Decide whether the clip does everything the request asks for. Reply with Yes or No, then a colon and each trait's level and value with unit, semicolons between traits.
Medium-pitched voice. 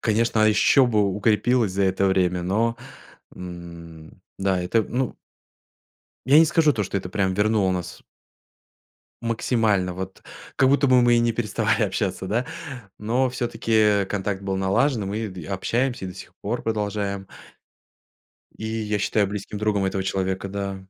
No: low, 105 Hz